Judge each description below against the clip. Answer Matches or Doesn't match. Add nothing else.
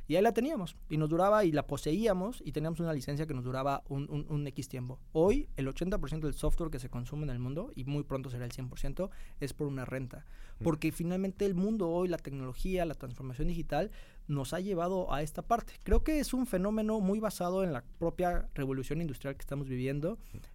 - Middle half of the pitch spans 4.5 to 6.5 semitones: Matches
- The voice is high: Doesn't match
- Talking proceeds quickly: Matches